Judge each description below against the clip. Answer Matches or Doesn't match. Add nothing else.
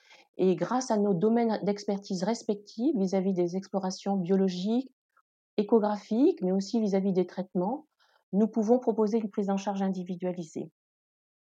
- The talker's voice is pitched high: Matches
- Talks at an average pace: Doesn't match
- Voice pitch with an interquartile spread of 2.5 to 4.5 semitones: Matches